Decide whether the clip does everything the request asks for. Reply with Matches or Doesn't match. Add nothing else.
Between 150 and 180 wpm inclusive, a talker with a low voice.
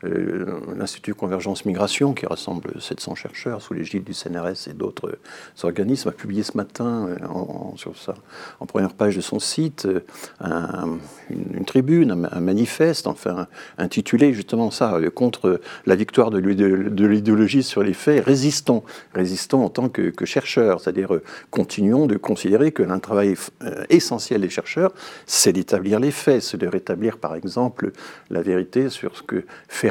Matches